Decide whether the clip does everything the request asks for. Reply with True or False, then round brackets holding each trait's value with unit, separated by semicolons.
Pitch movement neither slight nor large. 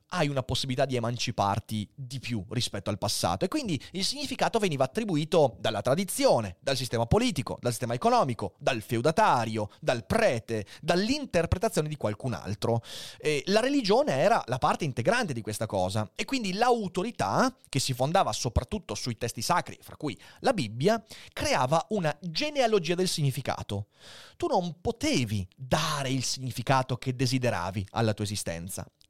False (8.5 semitones)